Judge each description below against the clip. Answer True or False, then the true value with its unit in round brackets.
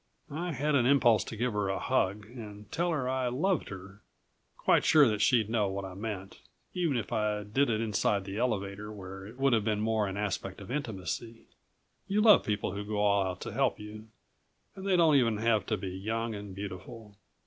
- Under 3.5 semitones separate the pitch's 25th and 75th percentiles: False (3.9 semitones)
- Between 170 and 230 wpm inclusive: True (205 wpm)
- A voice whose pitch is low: True (110 Hz)